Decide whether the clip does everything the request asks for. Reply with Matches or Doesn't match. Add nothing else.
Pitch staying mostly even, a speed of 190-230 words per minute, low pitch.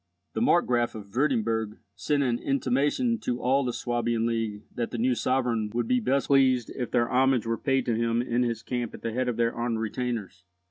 Matches